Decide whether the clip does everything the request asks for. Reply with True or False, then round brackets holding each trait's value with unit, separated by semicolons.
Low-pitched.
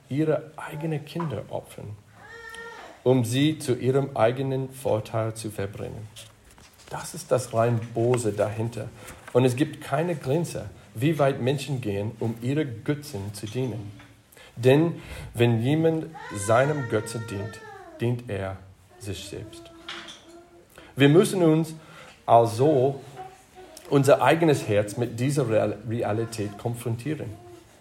True (125 Hz)